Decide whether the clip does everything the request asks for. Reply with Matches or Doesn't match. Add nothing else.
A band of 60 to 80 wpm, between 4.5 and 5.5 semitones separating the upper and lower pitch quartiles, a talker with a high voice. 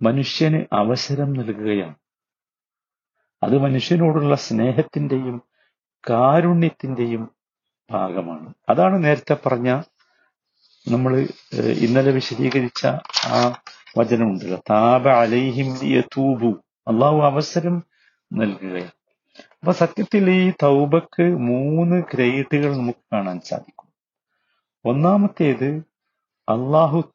Doesn't match